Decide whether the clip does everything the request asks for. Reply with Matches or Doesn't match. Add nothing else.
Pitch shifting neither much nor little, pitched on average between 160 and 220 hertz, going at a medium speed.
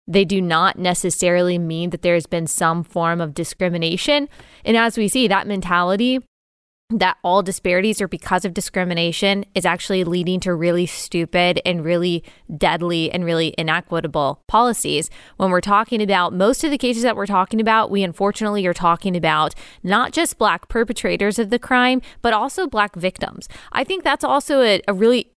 Matches